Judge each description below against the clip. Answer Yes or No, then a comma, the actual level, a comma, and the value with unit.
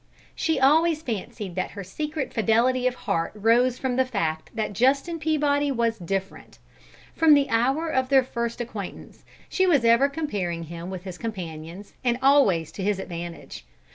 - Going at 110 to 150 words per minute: No, average, 165 wpm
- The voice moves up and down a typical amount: No, wide, 6.4 semitones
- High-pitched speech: Yes, high, 235 Hz